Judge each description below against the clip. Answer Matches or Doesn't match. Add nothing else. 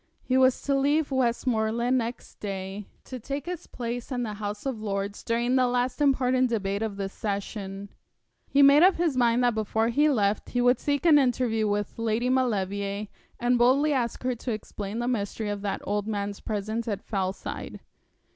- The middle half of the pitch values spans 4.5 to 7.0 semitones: Doesn't match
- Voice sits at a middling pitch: Doesn't match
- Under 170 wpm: Doesn't match